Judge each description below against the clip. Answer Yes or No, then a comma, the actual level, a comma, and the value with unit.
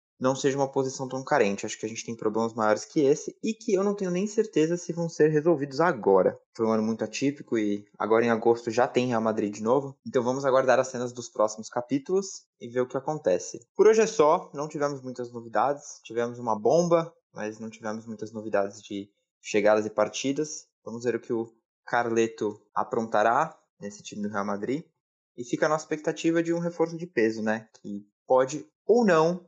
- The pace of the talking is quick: Yes, fast, 205 wpm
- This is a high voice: No, low, 125 Hz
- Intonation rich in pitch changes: Yes, wide, 6.3 semitones